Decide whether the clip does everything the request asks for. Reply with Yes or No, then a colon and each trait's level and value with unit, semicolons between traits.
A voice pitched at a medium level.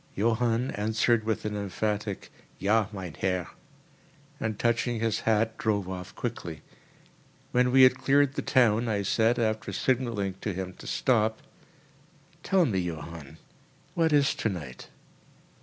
No: low, 110 Hz